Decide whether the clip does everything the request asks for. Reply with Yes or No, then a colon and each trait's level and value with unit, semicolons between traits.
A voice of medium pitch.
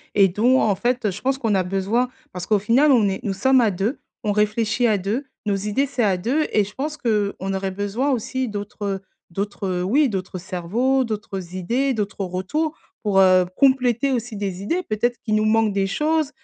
No: high, 210 Hz